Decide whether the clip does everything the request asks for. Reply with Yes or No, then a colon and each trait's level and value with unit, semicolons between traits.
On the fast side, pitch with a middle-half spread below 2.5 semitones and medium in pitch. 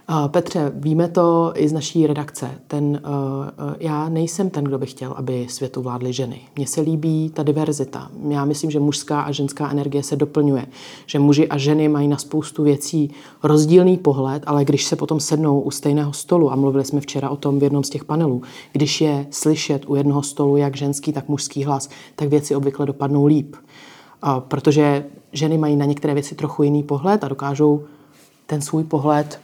Yes: fast, 195 wpm; narrow, 1.3 semitones; medium, 145 Hz